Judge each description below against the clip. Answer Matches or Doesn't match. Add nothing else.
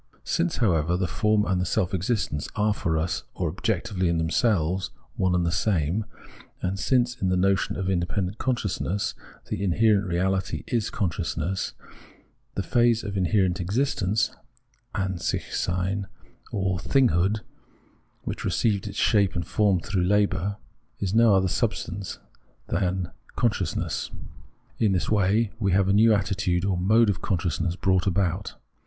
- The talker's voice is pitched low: Matches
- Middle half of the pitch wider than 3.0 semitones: Doesn't match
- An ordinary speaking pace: Matches